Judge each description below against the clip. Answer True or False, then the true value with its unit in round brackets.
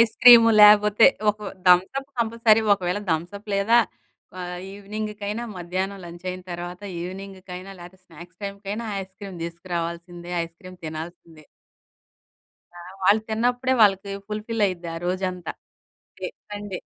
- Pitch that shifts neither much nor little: True (3.0 semitones)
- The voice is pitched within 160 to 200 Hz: True (190 Hz)